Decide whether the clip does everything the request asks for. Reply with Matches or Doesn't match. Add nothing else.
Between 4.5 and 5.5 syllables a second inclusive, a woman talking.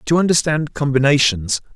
Doesn't match